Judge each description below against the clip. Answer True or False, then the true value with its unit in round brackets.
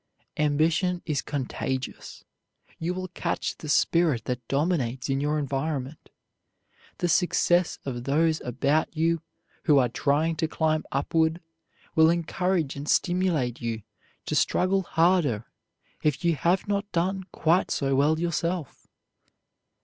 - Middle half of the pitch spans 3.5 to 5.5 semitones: True (3.9 semitones)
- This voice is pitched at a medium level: True (155 Hz)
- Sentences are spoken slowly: True (125 wpm)